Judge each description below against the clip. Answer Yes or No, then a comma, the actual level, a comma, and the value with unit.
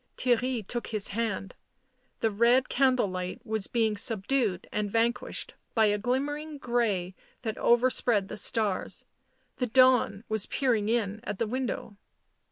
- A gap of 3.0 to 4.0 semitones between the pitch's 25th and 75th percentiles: Yes, average, 3.3 semitones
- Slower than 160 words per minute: Yes, average, 140 wpm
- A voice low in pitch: No, high, 225 Hz